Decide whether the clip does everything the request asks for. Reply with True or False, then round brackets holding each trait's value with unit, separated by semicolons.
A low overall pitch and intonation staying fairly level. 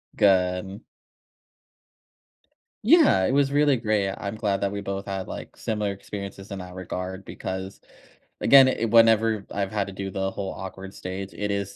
True (100 Hz; 2.1 semitones)